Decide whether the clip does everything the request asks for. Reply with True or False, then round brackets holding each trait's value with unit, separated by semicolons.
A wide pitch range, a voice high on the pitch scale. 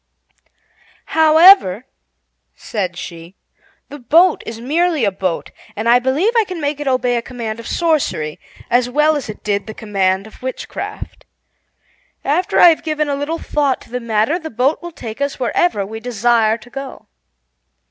True (6.0 semitones; 250 Hz)